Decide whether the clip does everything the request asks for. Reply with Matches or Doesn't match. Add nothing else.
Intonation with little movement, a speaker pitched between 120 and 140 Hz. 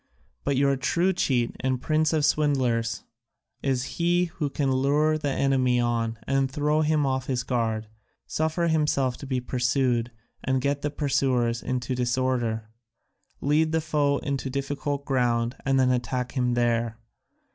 Doesn't match